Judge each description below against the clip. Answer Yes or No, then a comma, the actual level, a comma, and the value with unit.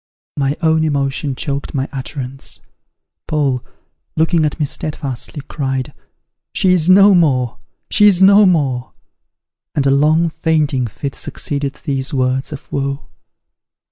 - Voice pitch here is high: No, medium, 145 Hz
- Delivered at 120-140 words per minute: Yes, slow, 135 wpm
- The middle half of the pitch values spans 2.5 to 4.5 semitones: Yes, average, 3.0 semitones